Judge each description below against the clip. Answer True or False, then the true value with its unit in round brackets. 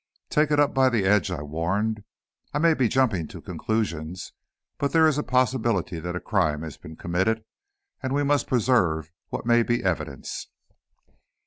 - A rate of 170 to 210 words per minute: True (175 wpm)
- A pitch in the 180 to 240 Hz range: False (110 Hz)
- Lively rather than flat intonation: True (7.2 semitones)